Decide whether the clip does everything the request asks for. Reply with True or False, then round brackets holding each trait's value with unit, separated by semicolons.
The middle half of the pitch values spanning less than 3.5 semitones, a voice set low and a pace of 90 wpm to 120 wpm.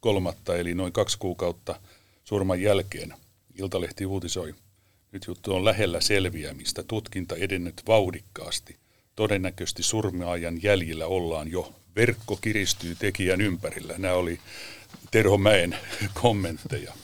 True (2.7 semitones; 95 Hz; 110 wpm)